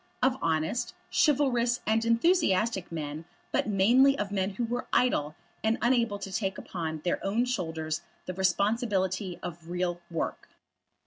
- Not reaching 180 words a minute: Yes, average, 140 wpm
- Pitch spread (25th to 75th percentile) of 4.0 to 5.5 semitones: Yes, average, 5.2 semitones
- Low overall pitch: No, high, 195 Hz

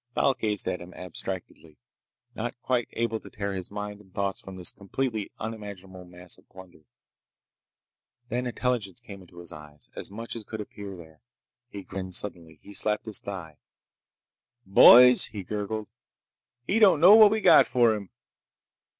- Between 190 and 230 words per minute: No, average, 160 wpm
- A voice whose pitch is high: No, low, 100 Hz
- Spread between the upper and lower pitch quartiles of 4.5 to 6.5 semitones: No, average, 3.8 semitones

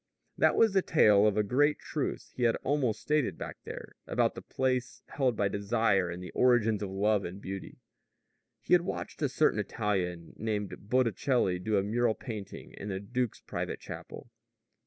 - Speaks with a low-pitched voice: Yes, low, 110 Hz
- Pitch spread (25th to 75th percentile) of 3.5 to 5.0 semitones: Yes, average, 4.3 semitones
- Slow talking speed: No, average, 180 wpm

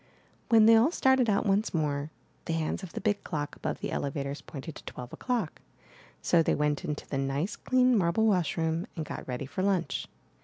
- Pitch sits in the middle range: Yes, medium, 170 Hz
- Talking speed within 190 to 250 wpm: Yes, average, 200 wpm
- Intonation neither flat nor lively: No, wide, 6.4 semitones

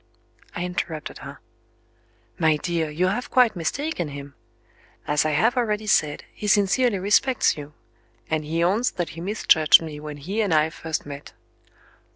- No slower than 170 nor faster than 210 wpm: No, average, 160 wpm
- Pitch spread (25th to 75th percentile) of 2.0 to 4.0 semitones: No, wide, 5.6 semitones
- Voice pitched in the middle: Yes, medium, 170 Hz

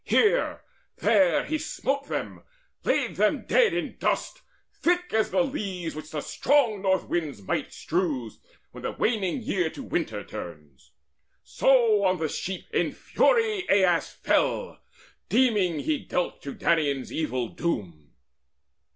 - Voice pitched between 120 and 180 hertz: No, high, 190 Hz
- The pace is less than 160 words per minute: Yes, slow, 135 wpm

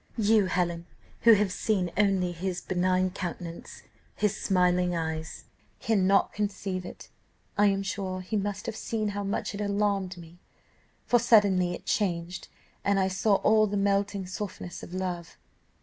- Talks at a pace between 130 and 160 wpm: Yes, average, 150 wpm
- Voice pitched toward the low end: No, high, 195 Hz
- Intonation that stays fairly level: Yes, narrow, 2.3 semitones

